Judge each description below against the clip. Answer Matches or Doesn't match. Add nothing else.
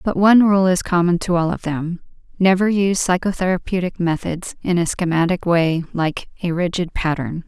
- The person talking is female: Matches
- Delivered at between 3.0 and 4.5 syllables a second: Doesn't match